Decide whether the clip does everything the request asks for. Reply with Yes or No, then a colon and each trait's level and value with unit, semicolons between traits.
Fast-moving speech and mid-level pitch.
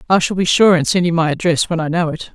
Yes: fast, 335 wpm; medium, 170 Hz